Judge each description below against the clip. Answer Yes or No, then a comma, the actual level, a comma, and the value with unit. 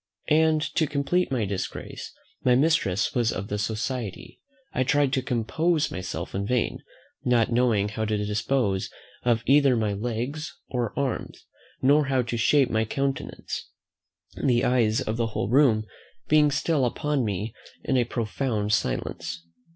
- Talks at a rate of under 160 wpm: Yes, average, 150 wpm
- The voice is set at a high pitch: No, low, 120 Hz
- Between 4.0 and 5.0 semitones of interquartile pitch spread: Yes, average, 4.4 semitones